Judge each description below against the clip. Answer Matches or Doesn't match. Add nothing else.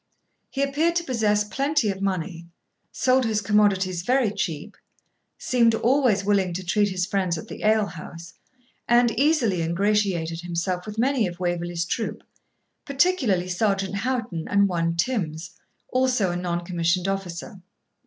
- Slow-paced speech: Doesn't match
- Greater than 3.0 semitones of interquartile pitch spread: Matches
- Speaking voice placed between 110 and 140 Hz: Doesn't match